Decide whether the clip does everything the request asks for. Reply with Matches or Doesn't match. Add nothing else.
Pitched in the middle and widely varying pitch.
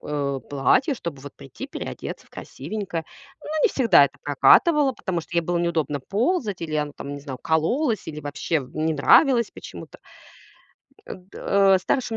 Matches